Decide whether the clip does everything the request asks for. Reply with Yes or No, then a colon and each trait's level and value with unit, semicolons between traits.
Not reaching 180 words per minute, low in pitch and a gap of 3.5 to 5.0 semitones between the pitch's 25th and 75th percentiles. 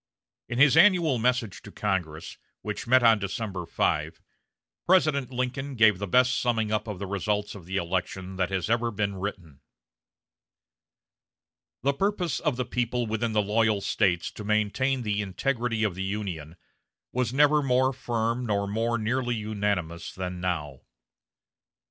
Yes: average, 150 wpm; low, 110 Hz; average, 4.5 semitones